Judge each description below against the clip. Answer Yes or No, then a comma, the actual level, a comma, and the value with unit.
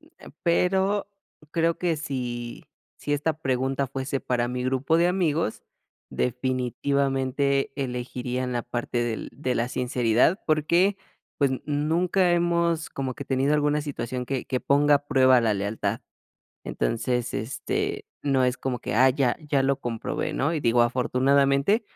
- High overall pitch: No, low, 135 Hz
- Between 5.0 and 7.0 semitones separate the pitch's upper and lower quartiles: No, average, 3.8 semitones